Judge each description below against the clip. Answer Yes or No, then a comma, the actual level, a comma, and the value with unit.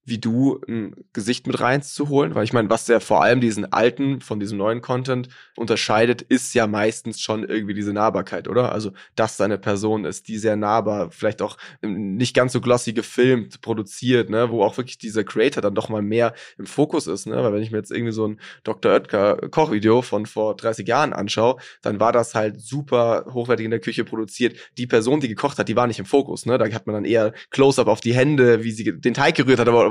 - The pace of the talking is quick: Yes, fast, 225 wpm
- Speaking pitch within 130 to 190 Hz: No, low, 115 Hz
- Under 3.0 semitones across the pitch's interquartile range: Yes, narrow, 2.4 semitones